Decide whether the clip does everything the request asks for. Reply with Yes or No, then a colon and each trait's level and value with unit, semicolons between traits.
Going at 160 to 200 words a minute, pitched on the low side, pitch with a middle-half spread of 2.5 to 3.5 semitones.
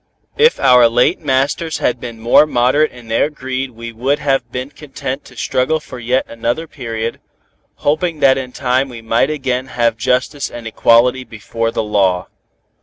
Yes: average, 170 wpm; low, 125 Hz; average, 2.8 semitones